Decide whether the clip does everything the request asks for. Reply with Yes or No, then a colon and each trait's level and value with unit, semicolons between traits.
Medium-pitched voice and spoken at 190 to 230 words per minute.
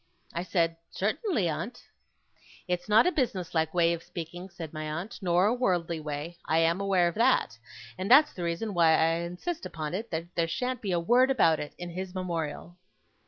Yes: medium, 175 Hz; average, 200 wpm